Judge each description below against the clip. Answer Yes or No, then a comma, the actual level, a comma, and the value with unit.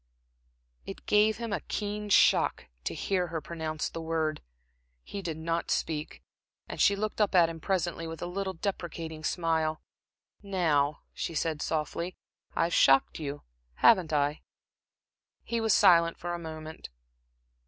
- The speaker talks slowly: No, average, 145 wpm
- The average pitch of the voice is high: No, medium, 165 Hz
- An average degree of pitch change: Yes, average, 3.3 semitones